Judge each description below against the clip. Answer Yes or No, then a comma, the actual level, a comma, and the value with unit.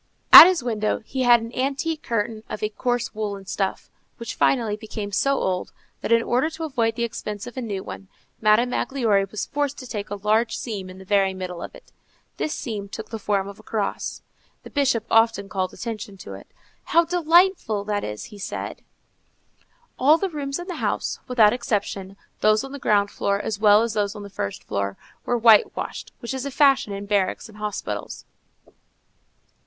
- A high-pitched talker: Yes, high, 220 Hz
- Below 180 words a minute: No, average, 195 wpm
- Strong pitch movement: No, average, 3.9 semitones